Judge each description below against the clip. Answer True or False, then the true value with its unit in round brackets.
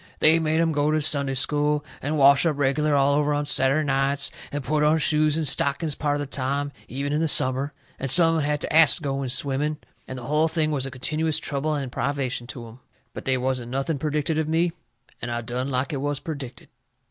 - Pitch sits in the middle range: True (145 Hz)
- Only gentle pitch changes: True (2.3 semitones)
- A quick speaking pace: True (235 wpm)